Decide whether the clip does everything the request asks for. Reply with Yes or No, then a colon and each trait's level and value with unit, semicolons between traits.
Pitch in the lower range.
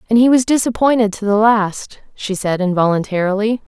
No: high, 215 Hz